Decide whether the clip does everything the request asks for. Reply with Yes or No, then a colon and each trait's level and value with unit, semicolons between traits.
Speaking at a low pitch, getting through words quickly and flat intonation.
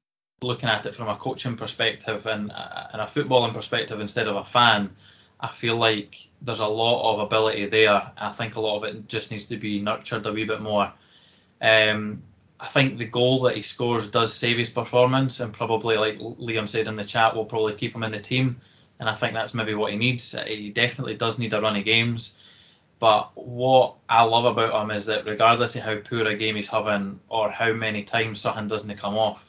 Yes: low, 110 Hz; fast, 220 wpm; narrow, 1.9 semitones